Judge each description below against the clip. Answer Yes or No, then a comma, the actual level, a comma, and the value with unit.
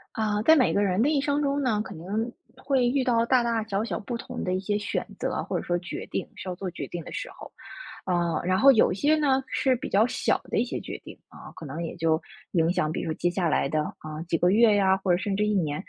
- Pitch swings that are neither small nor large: No, wide, 5.7 semitones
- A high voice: Yes, high, 205 Hz